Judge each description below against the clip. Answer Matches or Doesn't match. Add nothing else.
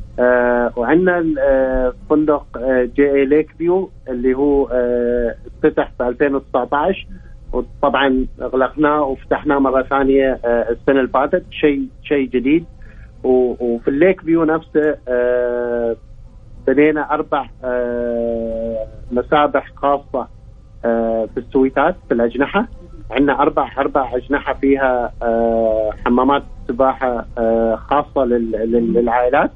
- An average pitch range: Matches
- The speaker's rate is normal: Matches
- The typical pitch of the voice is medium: Doesn't match